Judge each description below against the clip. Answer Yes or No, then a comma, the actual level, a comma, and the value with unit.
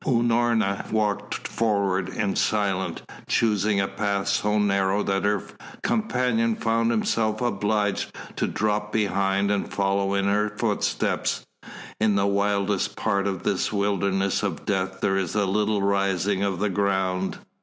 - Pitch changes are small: Yes, narrow, 1.6 semitones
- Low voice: Yes, low, 100 Hz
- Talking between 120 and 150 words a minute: Yes, average, 140 wpm